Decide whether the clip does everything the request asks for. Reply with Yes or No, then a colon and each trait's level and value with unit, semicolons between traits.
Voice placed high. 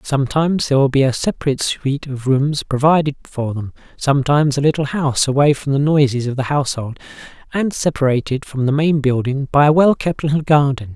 No: medium, 140 Hz